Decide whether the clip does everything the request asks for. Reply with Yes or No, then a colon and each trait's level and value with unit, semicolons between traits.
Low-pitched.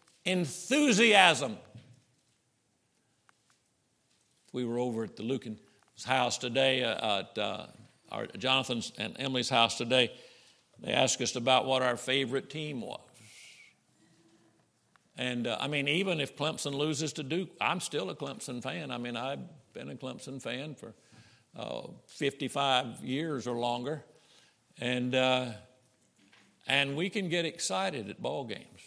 Yes: low, 130 Hz